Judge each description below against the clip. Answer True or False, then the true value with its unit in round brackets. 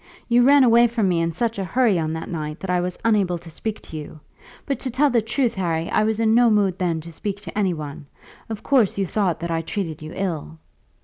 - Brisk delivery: True (250 wpm)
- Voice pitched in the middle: False (195 Hz)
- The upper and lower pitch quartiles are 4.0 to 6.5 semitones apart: True (5.5 semitones)